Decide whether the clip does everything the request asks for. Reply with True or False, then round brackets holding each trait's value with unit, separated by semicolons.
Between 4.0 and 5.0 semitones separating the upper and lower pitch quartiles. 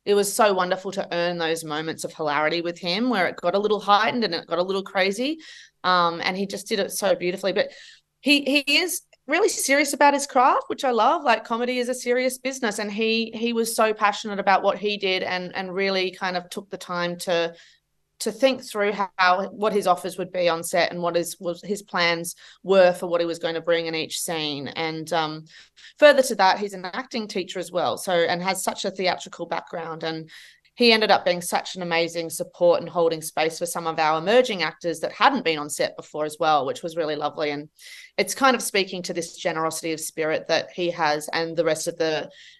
True (4.4 semitones)